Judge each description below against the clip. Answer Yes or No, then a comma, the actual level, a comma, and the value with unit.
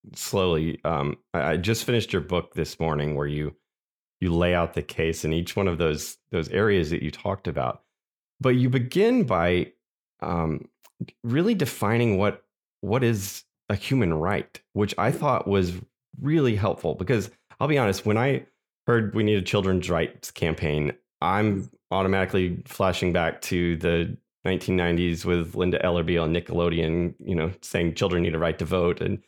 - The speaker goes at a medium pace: Yes, average, 165 wpm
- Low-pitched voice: Yes, very low, 90 Hz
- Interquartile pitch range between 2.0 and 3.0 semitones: No, average, 3.8 semitones